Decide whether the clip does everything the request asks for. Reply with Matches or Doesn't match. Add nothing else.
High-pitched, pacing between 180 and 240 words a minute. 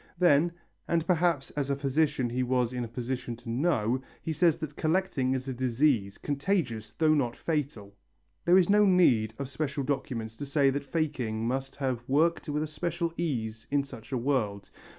Doesn't match